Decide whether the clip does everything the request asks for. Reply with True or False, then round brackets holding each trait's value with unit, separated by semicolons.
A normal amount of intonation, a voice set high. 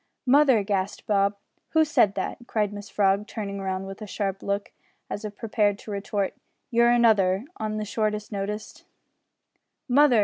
False (1.9 semitones; 210 Hz)